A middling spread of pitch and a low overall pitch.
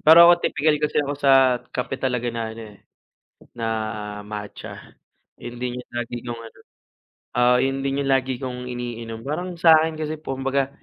Yes: average, 3.3 semitones; low, 130 Hz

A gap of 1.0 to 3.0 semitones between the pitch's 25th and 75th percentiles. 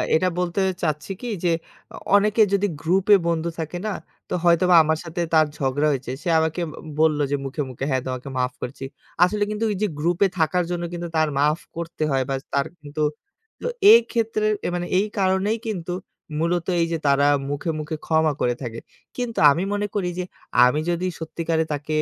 No: average, 3.8 semitones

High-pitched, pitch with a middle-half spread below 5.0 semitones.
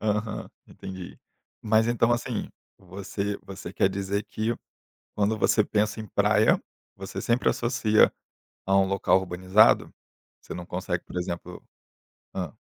No: low, 100 Hz; narrow, 2.6 semitones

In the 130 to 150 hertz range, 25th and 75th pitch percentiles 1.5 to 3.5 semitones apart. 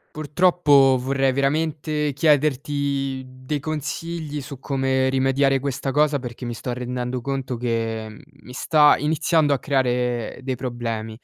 Yes: low, 135 Hz; average, 2.9 semitones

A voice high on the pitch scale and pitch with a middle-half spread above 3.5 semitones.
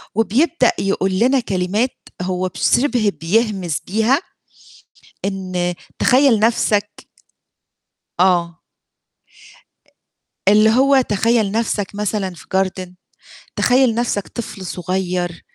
Yes: high, 205 Hz; average, 4.0 semitones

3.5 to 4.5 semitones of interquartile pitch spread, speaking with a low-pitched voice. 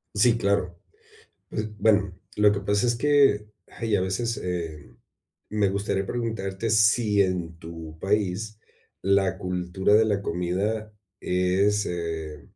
No: average, 2.9 semitones; low, 100 Hz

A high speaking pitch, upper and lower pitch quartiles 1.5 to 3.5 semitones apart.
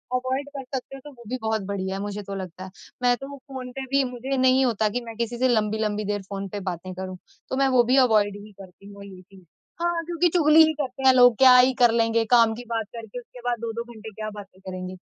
No: high, 230 Hz; average, 4.2 semitones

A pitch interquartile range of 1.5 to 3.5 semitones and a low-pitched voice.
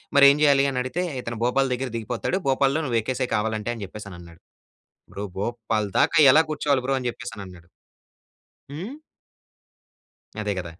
No: average, 4.4 semitones; low, 120 Hz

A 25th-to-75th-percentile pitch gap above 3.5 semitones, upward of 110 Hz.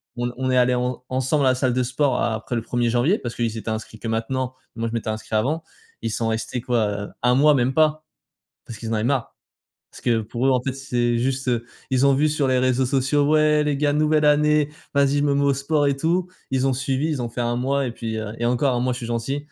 No: average, 3.1 semitones; low, 130 Hz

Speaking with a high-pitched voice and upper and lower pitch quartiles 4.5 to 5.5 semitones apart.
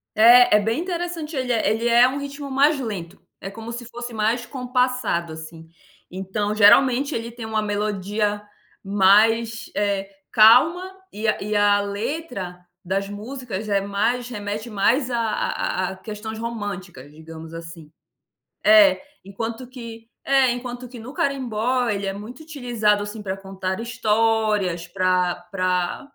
No: high, 220 Hz; average, 3.8 semitones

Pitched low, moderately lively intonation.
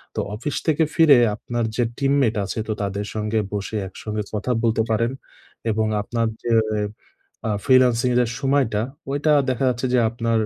Yes: low, 115 Hz; average, 3.0 semitones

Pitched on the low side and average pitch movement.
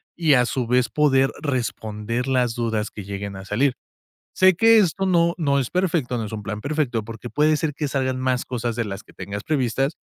Yes: low, 130 Hz; average, 5.0 semitones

